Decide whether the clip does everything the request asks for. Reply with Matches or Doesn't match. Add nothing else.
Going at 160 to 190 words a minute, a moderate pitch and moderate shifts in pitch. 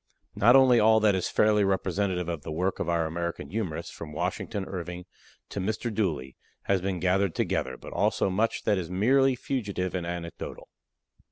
Doesn't match